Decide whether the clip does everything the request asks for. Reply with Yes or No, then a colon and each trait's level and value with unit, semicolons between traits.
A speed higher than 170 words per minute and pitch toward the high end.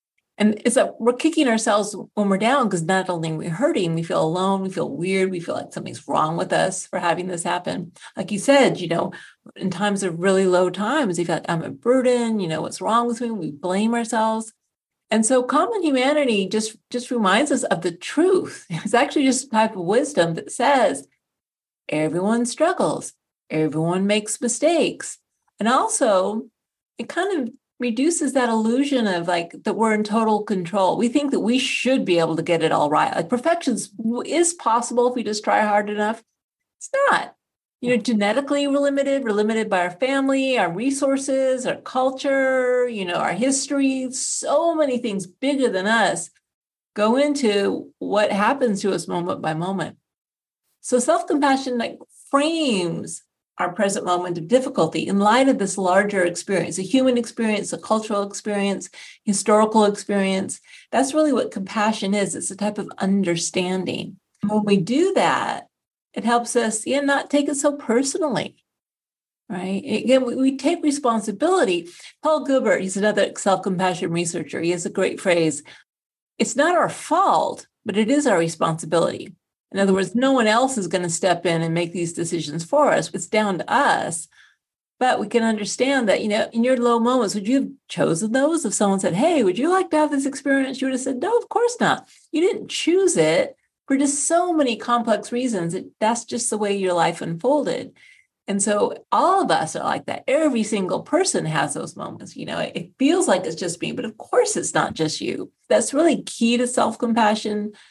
Yes: average, 185 wpm; high, 225 Hz